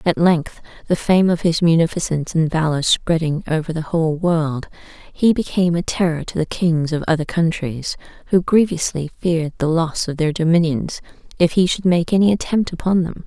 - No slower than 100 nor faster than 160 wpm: No, average, 180 wpm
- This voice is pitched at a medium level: Yes, medium, 165 Hz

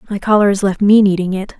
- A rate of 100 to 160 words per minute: No, fast, 265 wpm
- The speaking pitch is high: Yes, high, 200 Hz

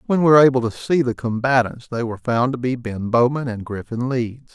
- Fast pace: Yes, fast, 240 wpm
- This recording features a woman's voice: No, male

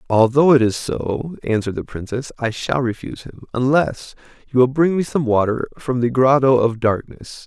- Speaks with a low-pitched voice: Yes, low, 125 Hz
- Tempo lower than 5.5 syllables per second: Yes, 5.0 syllables/s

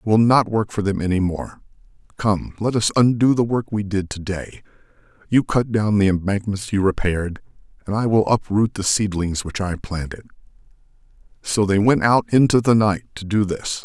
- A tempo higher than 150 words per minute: Yes, average, 185 wpm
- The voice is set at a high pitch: No, low, 105 Hz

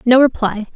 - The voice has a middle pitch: No, high, 240 Hz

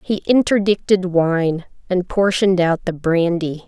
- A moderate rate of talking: No, slow, 130 wpm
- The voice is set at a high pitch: No, medium, 180 Hz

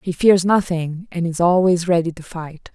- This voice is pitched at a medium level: Yes, medium, 175 Hz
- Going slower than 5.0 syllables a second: Yes, 4.6 syllables/s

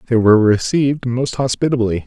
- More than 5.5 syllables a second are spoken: Yes, 5.9 syllables/s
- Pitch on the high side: No, low, 120 Hz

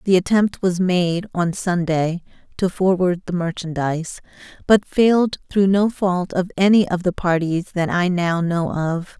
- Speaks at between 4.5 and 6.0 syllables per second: No, 4.3 syllables/s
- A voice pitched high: No, medium, 180 Hz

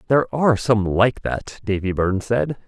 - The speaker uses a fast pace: No, average, 180 wpm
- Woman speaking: No, male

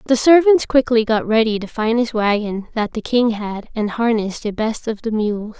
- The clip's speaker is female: Yes, female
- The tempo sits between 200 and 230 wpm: Yes, fast, 205 wpm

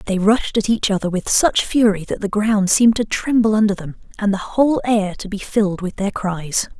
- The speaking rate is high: Yes, fast, 230 wpm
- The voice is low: No, high, 205 Hz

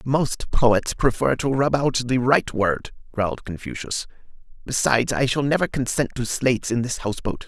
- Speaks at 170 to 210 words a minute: Yes, average, 175 wpm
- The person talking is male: Yes, male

